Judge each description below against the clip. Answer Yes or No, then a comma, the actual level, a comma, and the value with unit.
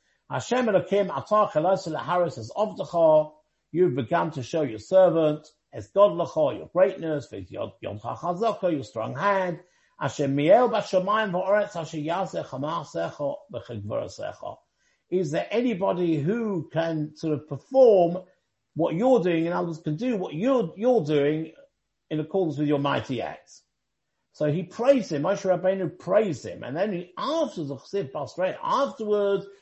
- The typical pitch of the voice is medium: Yes, medium, 175 Hz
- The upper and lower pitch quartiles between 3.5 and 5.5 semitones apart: Yes, average, 4.7 semitones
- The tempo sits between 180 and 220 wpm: No, average, 150 wpm